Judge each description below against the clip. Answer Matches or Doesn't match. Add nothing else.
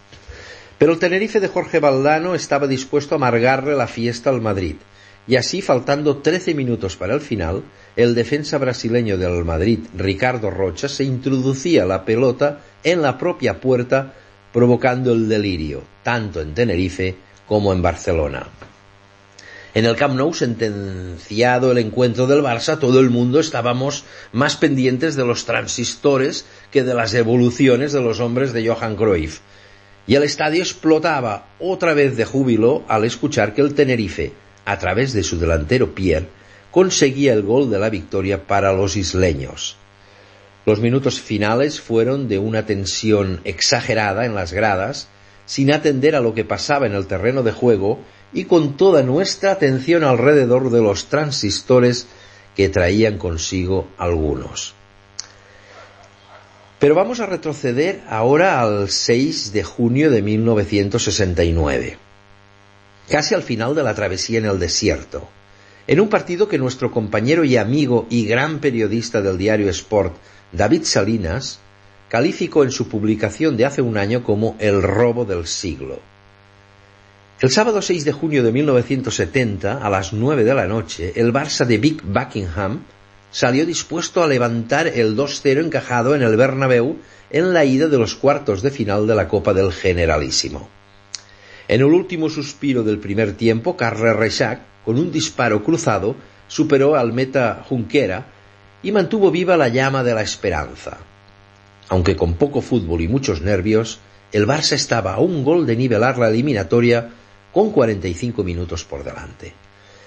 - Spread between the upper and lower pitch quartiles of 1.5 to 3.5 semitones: Doesn't match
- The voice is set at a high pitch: Doesn't match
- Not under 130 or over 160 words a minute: Matches